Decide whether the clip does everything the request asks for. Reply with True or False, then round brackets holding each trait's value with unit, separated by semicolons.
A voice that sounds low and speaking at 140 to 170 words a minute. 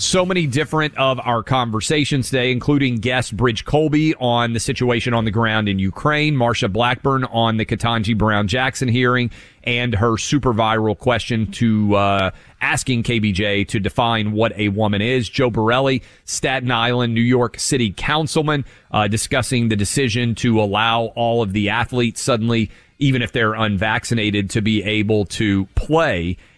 True (115 Hz; 160 wpm)